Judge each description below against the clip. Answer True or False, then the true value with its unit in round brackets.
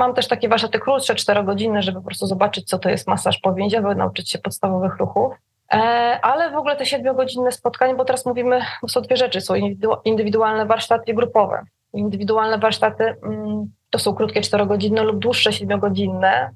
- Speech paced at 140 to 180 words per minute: True (160 wpm)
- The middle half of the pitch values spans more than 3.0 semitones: True (3.4 semitones)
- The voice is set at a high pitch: True (220 Hz)